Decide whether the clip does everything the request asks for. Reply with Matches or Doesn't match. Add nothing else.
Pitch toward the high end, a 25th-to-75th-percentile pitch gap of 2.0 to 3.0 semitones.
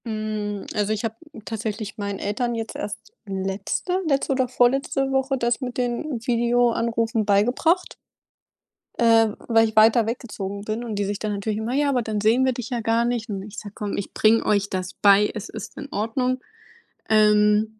Matches